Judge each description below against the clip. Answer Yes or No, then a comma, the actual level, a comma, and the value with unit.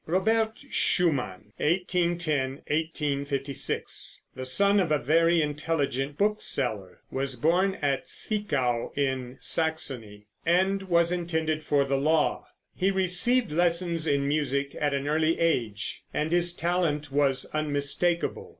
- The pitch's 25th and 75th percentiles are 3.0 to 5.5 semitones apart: Yes, average, 3.9 semitones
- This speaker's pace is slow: Yes, slow, 125 wpm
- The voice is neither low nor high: Yes, medium, 155 Hz